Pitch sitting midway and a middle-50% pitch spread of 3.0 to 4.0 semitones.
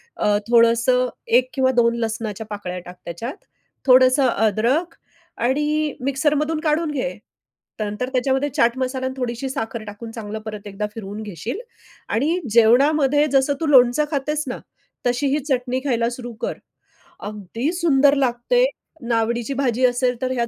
No: very high, 250 Hz; average, 3.4 semitones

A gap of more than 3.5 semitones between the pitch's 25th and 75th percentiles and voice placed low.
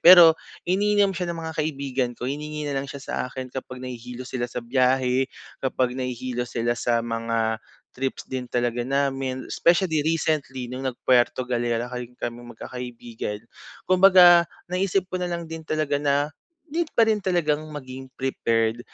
Yes: average, 4.7 semitones; low, 130 Hz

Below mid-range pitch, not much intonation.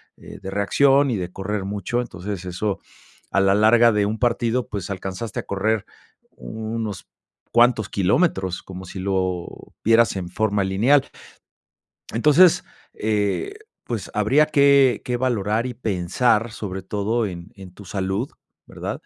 No: low, 105 Hz; average, 3.7 semitones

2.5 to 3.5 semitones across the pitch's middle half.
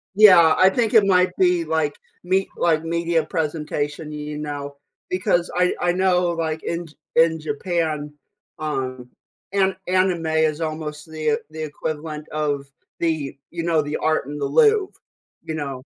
Yes: average, 2.8 semitones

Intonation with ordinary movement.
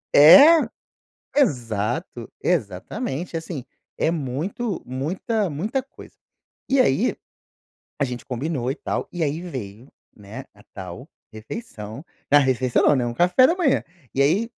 No: wide, 7.2 semitones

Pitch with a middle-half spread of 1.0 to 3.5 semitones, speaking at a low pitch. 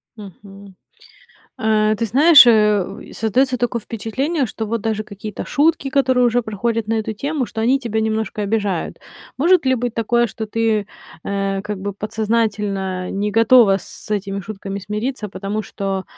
No: average, 2.8 semitones; high, 220 Hz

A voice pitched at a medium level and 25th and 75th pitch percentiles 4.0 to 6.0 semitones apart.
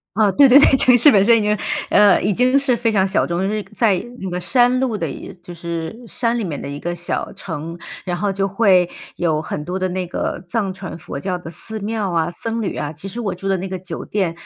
No: high, 195 Hz; average, 4.3 semitones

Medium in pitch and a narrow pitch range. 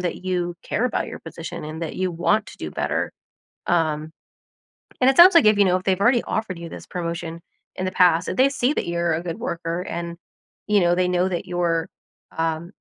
Yes: medium, 175 Hz; narrow, 2.3 semitones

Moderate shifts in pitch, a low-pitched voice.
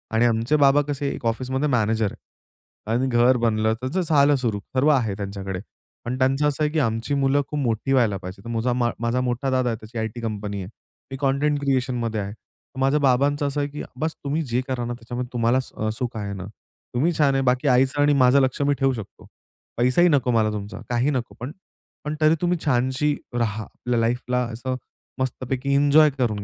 Yes: average, 3.4 semitones; low, 125 Hz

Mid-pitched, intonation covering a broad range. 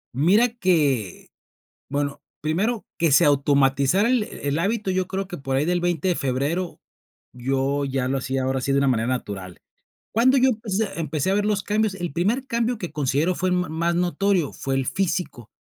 Yes: medium, 170 Hz; wide, 6.3 semitones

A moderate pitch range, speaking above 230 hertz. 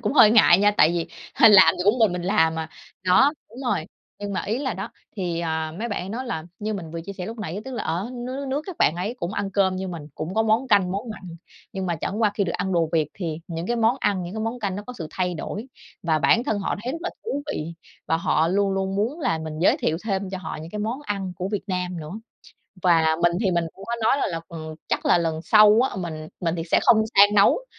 No: average, 4.4 semitones; high, 195 Hz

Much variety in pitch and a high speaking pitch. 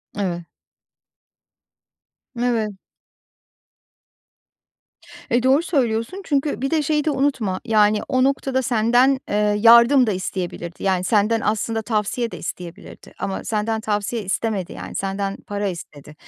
No: average, 4.2 semitones; high, 220 Hz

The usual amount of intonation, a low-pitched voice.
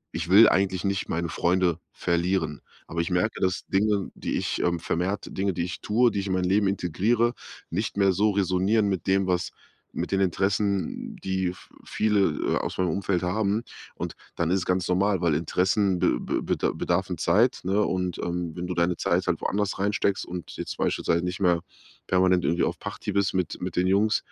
No: narrow, 2.1 semitones; very low, 95 Hz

